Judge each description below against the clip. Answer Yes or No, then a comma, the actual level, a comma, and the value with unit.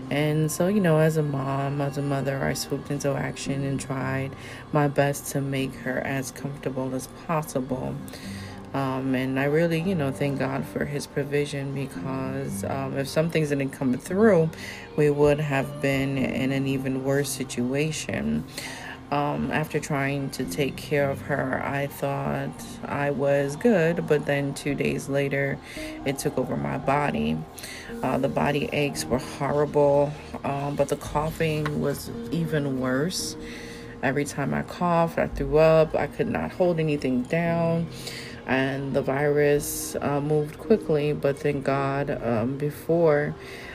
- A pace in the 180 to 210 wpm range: No, average, 155 wpm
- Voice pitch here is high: No, medium, 140 Hz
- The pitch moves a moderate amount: No, narrow, 1.9 semitones